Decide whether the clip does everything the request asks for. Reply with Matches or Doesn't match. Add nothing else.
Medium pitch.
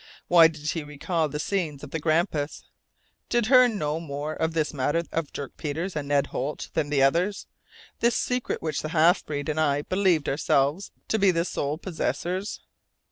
Matches